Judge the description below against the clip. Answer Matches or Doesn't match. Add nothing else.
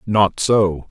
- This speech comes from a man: Matches